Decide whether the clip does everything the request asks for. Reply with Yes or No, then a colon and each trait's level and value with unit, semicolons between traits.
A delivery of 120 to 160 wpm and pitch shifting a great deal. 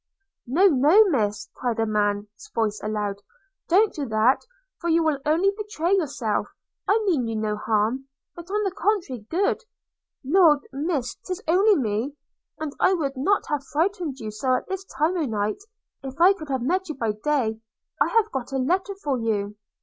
No: average, 180 wpm; wide, 8.3 semitones